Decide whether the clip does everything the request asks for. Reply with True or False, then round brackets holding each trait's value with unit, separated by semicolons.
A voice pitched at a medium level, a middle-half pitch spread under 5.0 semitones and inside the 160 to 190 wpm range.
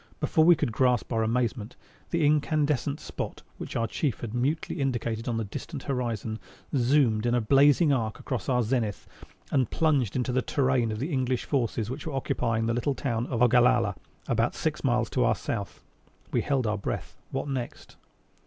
False (125 Hz; 3.2 semitones; 180 wpm)